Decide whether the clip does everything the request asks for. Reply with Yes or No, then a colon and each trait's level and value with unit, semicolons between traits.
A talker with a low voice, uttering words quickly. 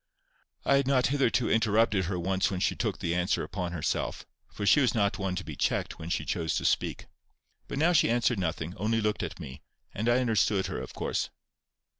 Yes: low, 100 Hz; fast, 210 wpm